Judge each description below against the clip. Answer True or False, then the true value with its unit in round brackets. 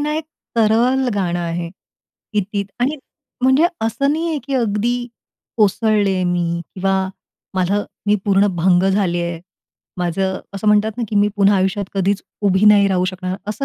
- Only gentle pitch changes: False (3.2 semitones)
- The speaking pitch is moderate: False (200 Hz)